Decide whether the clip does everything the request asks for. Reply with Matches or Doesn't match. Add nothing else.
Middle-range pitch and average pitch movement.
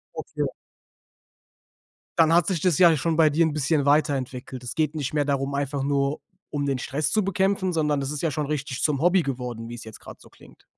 Matches